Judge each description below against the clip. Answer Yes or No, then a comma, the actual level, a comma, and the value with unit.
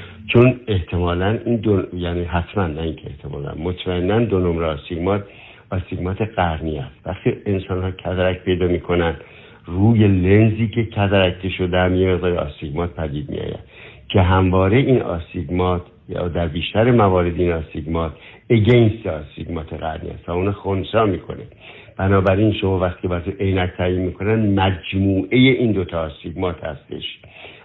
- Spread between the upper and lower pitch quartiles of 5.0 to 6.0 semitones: No, average, 2.7 semitones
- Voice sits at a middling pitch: No, very low, 95 Hz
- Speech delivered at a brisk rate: No, average, 145 wpm